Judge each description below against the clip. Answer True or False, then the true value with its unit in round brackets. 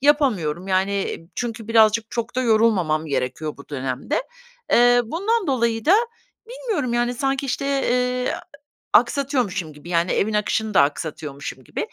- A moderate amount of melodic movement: False (6.8 semitones)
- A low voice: False (225 Hz)